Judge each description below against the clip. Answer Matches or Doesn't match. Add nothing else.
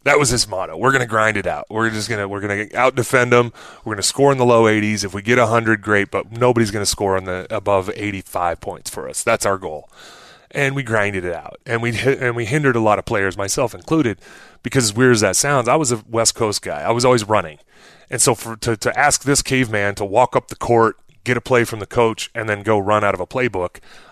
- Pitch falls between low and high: Doesn't match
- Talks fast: Matches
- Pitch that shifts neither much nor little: Matches